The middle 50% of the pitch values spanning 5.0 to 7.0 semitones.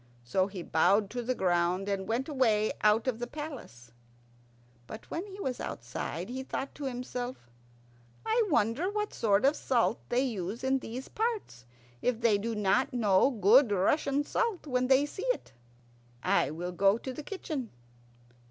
Yes: wide, 5.5 semitones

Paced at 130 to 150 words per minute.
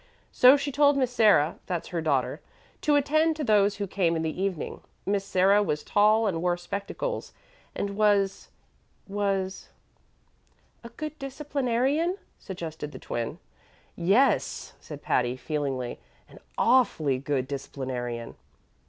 Yes: slow, 135 wpm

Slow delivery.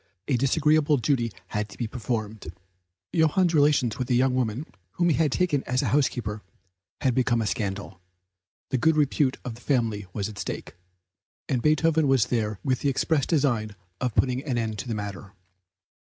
No: average, 175 wpm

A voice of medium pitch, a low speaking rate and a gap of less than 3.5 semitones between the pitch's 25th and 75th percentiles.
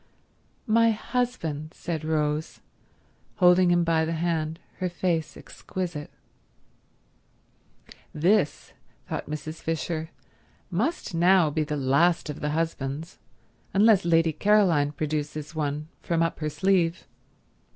Yes: medium, 165 Hz; slow, 110 wpm; average, 2.8 semitones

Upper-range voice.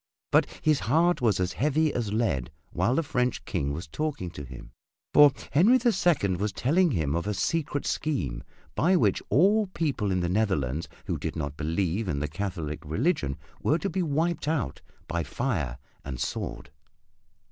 No: low, 105 Hz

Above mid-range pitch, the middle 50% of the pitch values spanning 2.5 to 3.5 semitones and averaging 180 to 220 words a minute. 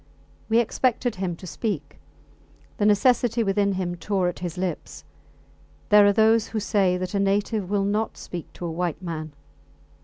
No: high, 200 Hz; average, 3.2 semitones; average, 165 wpm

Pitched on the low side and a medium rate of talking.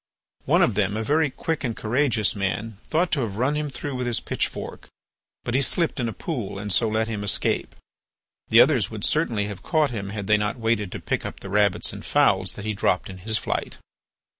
No: low, 110 Hz; fast, 220 wpm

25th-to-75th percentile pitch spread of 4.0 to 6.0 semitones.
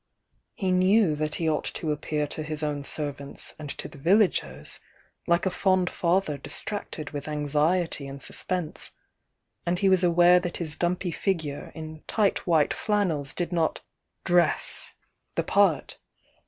No: average, 3.3 semitones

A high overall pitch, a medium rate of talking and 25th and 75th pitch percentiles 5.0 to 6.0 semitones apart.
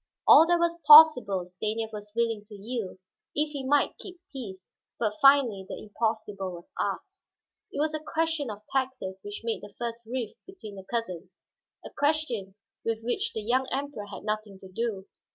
Yes: high, 230 Hz; average, 175 wpm; wide, 5.6 semitones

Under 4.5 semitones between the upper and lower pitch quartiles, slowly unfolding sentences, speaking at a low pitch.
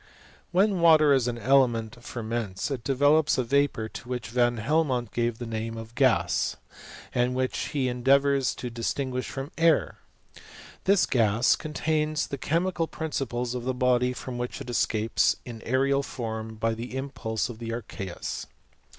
No: average, 3.2 semitones; average, 160 wpm; low, 125 Hz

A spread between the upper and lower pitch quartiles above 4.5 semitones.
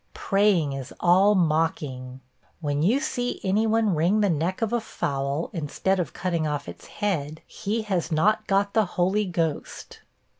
Yes: average, 5.1 semitones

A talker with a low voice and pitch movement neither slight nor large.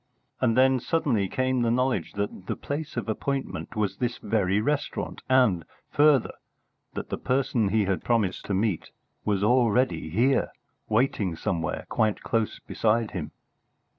Yes: low, 115 Hz; average, 4.4 semitones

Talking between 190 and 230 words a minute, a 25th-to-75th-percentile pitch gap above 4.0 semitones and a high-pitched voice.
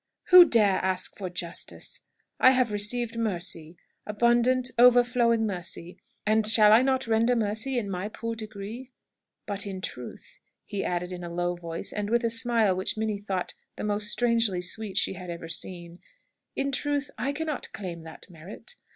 No: average, 170 wpm; average, 4.5 semitones; high, 210 Hz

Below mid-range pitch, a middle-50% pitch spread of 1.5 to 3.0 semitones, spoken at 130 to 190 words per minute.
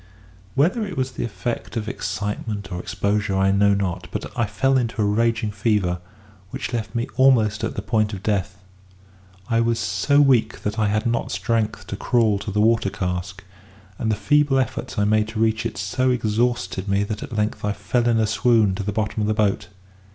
No: low, 105 Hz; narrow, 2.6 semitones; fast, 205 wpm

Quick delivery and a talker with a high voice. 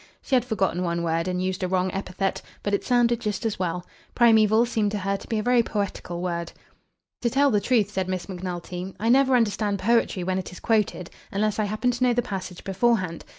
Yes: fast, 220 wpm; high, 200 Hz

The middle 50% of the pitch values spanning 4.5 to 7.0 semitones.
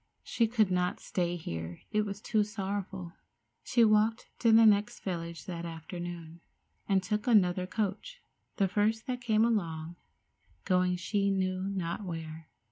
No: average, 3.5 semitones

